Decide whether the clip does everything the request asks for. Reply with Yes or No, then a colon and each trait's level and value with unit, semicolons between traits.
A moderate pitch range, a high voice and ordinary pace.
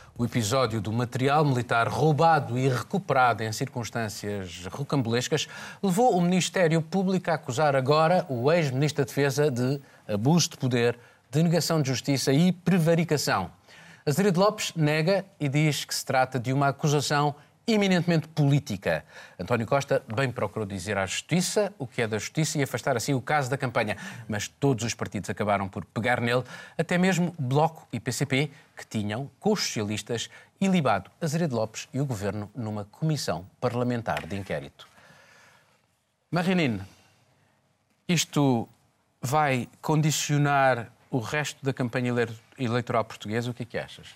No: average, 4.7 semitones; low, 135 Hz; average, 145 wpm